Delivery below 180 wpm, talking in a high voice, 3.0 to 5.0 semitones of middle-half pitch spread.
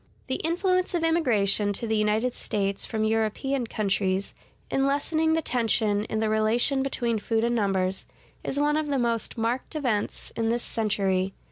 Yes: average, 165 wpm; high, 225 Hz; average, 4.5 semitones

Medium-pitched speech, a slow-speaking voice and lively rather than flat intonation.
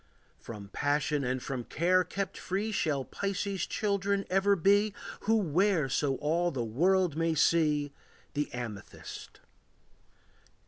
Yes: medium, 165 Hz; slow, 125 wpm; wide, 5.7 semitones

